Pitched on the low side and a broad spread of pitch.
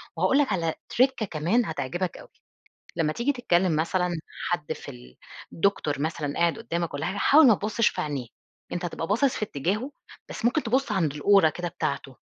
No: medium, 175 Hz; wide, 6.5 semitones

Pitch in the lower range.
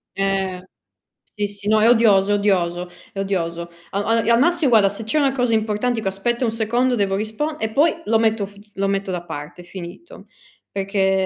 No: high, 205 Hz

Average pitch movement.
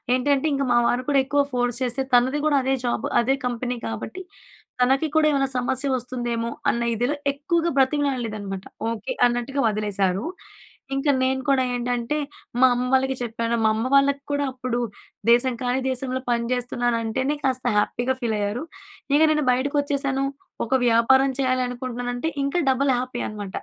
No: narrow, 2.3 semitones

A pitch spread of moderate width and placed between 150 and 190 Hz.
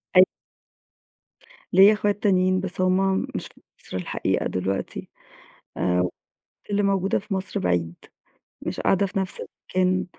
No: narrow, 1.8 semitones; medium, 185 Hz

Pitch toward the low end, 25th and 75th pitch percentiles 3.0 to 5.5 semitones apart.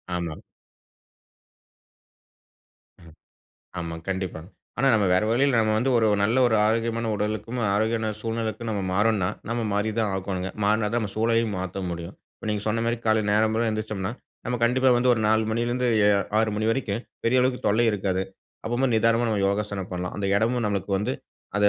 No: low, 110 Hz; narrow, 2.5 semitones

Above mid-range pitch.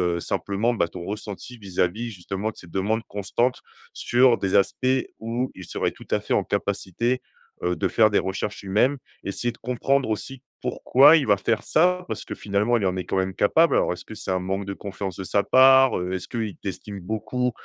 No: low, 105 Hz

